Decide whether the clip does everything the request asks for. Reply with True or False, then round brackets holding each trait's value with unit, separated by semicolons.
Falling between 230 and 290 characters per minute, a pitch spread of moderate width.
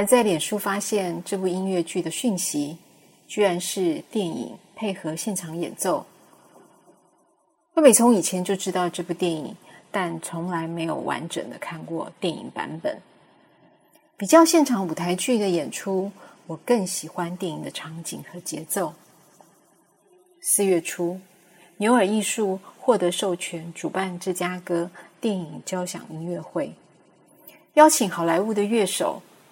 False (210 characters per minute; 4.0 semitones)